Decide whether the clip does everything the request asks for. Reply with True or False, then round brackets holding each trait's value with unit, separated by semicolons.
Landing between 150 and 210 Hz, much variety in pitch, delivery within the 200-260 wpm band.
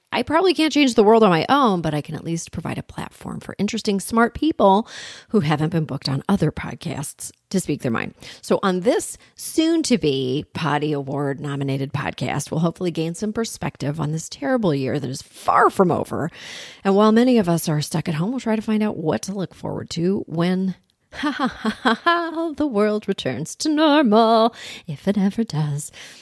True (190 Hz; 7.1 semitones; 205 wpm)